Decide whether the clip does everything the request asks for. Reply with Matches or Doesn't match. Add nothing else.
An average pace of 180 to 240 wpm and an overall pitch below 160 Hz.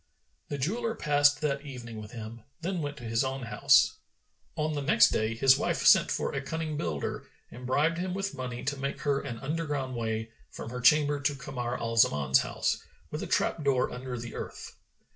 Matches